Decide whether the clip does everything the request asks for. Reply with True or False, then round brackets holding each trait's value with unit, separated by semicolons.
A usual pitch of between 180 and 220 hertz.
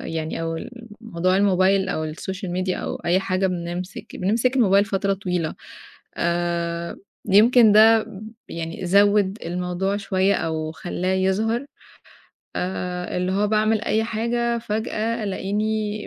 True (190 Hz)